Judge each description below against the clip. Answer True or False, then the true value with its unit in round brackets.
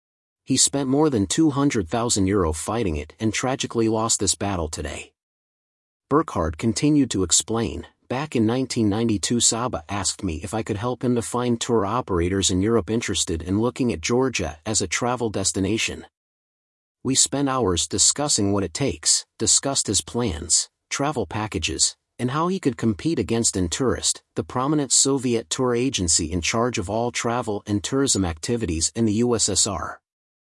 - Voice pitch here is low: True (110 Hz)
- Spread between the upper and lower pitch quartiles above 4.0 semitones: True (4.4 semitones)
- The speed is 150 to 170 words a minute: True (155 wpm)